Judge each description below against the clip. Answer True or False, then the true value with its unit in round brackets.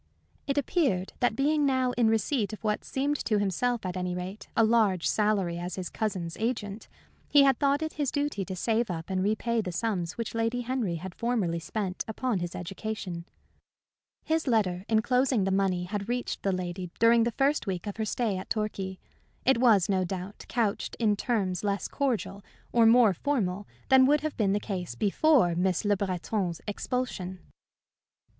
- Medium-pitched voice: False (210 Hz)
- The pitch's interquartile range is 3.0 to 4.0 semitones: False (4.7 semitones)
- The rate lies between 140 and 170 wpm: False (180 wpm)